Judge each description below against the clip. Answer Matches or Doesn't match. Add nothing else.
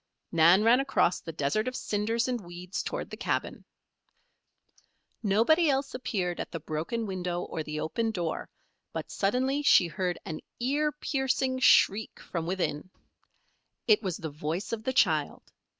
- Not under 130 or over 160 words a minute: Matches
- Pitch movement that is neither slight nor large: Doesn't match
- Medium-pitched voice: Doesn't match